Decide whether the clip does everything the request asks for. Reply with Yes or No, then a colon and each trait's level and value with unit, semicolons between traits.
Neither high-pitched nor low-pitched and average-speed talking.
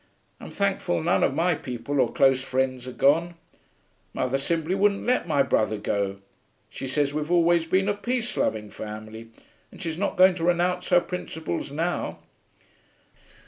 Yes: medium, 155 Hz; average, 160 wpm